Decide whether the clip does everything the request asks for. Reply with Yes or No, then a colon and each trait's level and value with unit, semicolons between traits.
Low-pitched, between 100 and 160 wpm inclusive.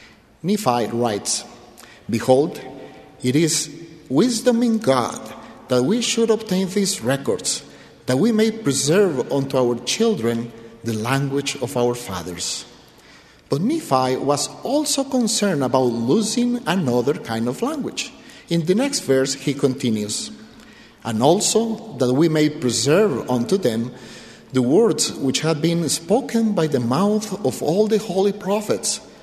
No: medium, 150 Hz; slow, 135 wpm